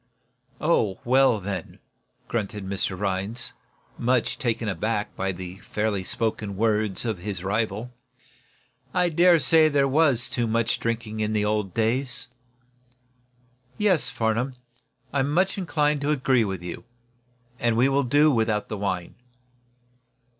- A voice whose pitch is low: Yes, low, 115 Hz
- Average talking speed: No, slow, 130 wpm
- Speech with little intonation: No, average, 4.7 semitones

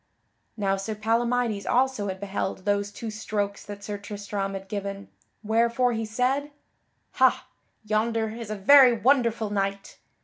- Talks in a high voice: Yes, high, 215 Hz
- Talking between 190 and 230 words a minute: No, average, 140 wpm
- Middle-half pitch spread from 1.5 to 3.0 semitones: Yes, narrow, 2.5 semitones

